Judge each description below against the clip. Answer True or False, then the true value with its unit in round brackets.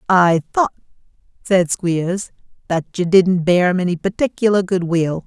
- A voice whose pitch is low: False (180 Hz)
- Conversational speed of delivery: True (150 wpm)